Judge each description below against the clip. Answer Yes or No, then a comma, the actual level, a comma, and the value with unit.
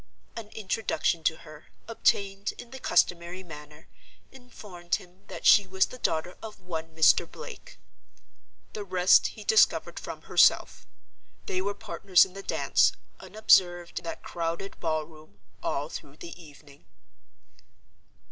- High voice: No, medium, 180 Hz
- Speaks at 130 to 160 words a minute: Yes, average, 140 wpm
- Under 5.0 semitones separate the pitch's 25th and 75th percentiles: Yes, average, 3.6 semitones